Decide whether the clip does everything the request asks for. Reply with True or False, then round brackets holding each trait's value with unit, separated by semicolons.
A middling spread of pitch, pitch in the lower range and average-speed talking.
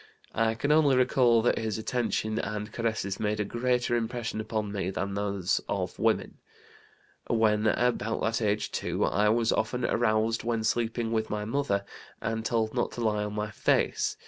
False (1.9 semitones; 110 Hz; 170 wpm)